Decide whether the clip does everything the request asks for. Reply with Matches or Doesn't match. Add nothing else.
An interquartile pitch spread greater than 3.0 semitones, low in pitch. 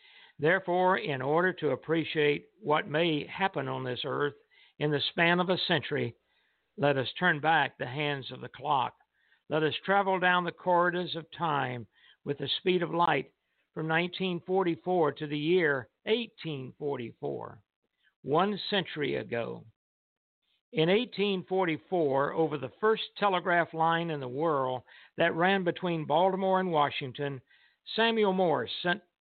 Doesn't match